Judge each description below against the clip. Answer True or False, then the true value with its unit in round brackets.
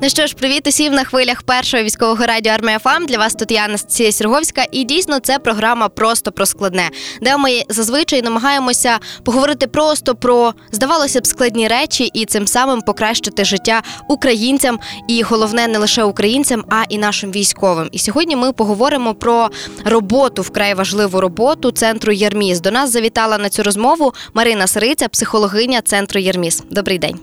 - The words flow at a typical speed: False (165 wpm)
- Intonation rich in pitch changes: False (3.7 semitones)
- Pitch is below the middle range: False (230 Hz)